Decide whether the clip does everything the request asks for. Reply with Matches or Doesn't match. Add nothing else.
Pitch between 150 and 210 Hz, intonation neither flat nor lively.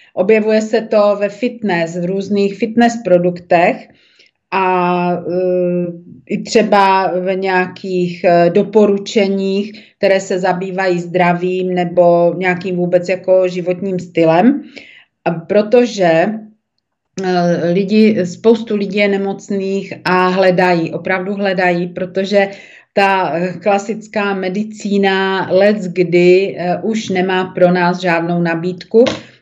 Doesn't match